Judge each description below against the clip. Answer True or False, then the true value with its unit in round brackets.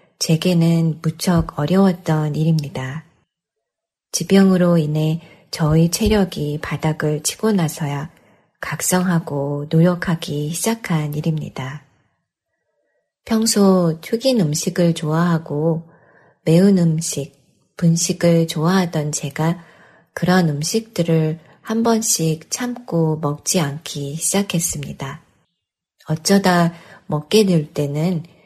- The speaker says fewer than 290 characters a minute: True (210 characters per minute)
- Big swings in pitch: False (2.9 semitones)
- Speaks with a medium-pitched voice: True (165 Hz)